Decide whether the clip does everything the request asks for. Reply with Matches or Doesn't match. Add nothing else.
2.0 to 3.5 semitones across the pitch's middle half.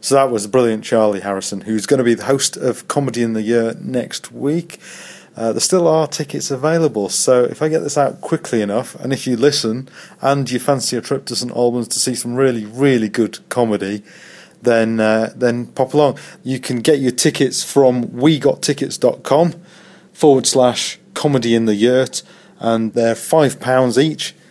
Doesn't match